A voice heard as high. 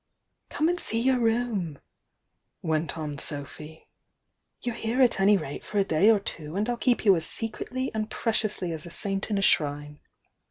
Yes: high, 200 Hz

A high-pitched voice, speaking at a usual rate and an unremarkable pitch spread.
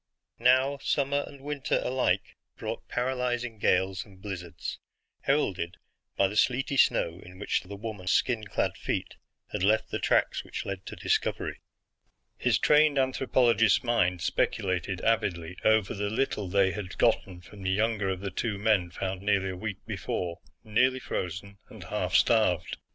No: low, 105 Hz; average, 155 wpm; average, 4.7 semitones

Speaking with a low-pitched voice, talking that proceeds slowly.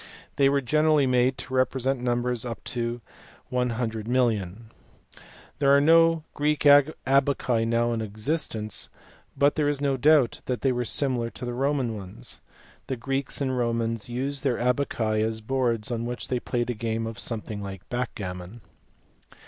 No: low, 125 Hz; average, 150 wpm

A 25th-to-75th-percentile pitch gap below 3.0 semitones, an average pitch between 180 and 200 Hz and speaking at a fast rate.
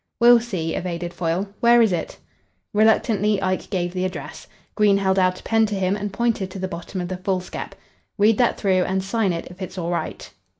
Yes: narrow, 2.5 semitones; high, 190 Hz; fast, 210 wpm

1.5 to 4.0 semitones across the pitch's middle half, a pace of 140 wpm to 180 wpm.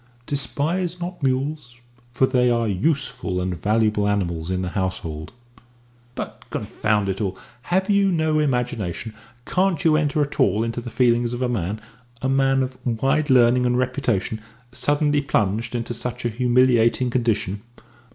No: average, 4.7 semitones; average, 150 wpm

